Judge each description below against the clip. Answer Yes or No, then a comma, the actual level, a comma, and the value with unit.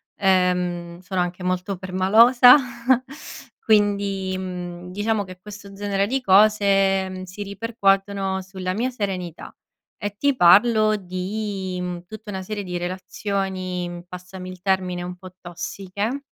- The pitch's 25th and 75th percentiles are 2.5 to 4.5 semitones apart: No, narrow, 2.1 semitones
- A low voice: No, high, 190 Hz